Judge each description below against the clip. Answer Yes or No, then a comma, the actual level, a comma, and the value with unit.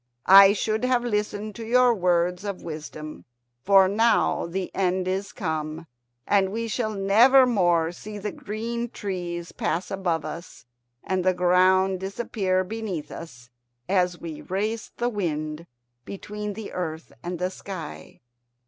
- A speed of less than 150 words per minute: Yes, average, 140 wpm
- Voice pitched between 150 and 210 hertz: Yes, high, 190 Hz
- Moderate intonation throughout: Yes, average, 3.3 semitones